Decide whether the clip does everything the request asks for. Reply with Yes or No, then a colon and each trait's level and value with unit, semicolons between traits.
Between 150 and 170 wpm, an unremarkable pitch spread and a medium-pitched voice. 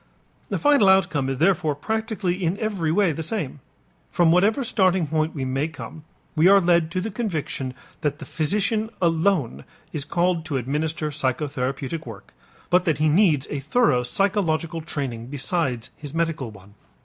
Yes: average, 160 wpm; average, 4.7 semitones; medium, 160 Hz